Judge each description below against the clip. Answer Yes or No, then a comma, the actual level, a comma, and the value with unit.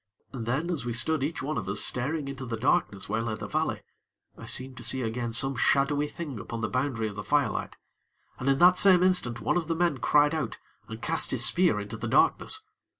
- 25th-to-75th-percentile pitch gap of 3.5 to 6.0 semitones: Yes, average, 4.9 semitones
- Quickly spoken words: Yes, fast, 225 wpm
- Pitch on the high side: No, low, 135 Hz